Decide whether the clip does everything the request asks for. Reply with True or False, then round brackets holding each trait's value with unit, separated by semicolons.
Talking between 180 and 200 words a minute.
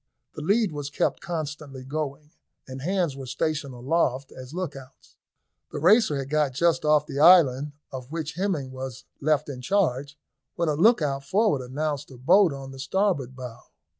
False (165 wpm)